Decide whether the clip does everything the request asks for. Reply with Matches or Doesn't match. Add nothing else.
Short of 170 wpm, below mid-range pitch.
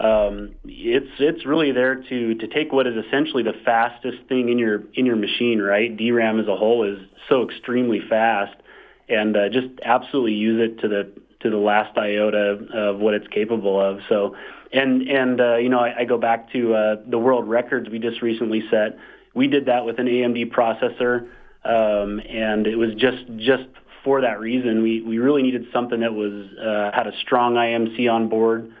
Doesn't match